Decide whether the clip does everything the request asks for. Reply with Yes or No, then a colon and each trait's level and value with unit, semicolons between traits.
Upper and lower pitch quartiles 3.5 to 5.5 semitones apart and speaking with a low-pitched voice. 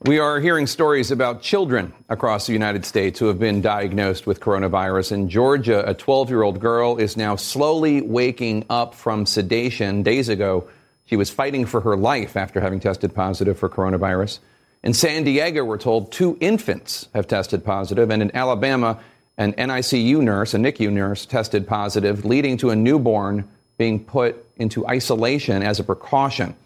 Yes: average, 4.1 semitones; low, 115 Hz